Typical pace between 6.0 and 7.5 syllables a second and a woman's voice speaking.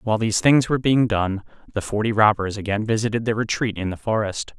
No: 6.2 syllables/s; male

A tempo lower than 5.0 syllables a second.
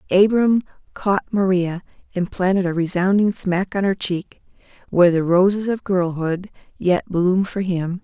Yes: 4.5 syllables/s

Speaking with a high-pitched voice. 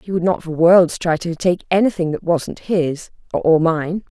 No: medium, 170 Hz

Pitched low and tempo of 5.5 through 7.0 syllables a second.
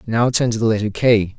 Yes: low, 110 Hz; 5.6 syllables/s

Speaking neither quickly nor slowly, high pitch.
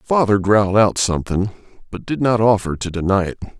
No: average, 185 wpm; low, 105 Hz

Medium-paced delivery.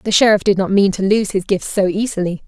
No: fast, 265 wpm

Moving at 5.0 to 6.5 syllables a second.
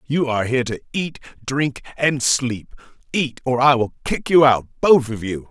No: 4.7 syllables/s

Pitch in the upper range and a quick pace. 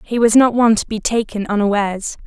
Yes: high, 220 Hz; fast, 210 wpm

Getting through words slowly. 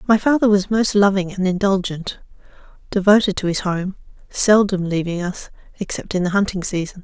No: average, 160 wpm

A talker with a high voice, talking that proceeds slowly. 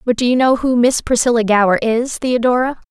No: high, 240 Hz; fast, 205 wpm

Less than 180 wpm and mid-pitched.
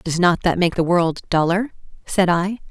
No: average, 200 wpm; medium, 175 Hz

